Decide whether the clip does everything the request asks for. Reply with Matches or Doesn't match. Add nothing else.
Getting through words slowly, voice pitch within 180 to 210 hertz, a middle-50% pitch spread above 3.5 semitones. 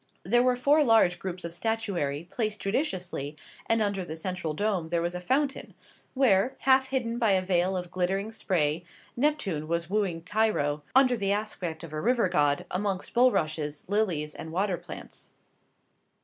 Doesn't match